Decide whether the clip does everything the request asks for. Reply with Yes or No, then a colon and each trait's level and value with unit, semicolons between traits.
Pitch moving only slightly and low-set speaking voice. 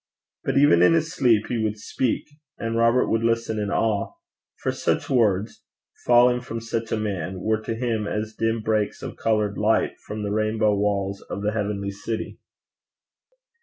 Yes: narrow, 1.8 semitones; low, 110 Hz